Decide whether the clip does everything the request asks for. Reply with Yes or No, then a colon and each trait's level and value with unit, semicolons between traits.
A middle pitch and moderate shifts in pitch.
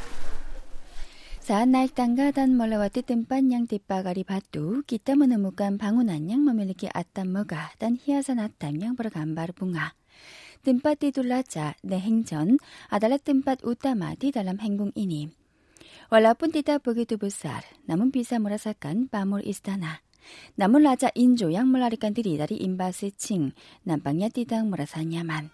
No: high, 220 Hz; average, 5.0 semitones